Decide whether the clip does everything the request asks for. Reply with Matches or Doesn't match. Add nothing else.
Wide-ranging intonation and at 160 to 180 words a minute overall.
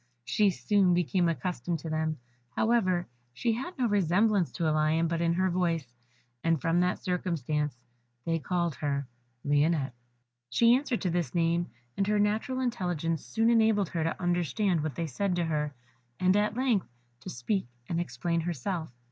Doesn't match